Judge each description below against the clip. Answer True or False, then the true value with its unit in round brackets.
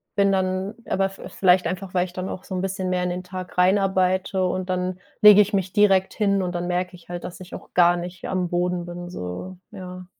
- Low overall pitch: False (185 Hz)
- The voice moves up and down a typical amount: False (1.1 semitones)